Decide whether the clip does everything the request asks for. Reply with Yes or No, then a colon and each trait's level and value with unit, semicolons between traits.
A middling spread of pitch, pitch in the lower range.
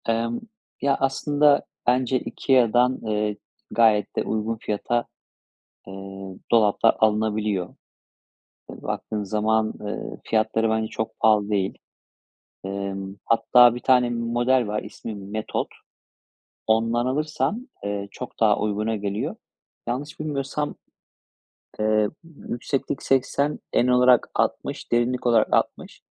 Yes: average, 3.0 semitones; low, 115 Hz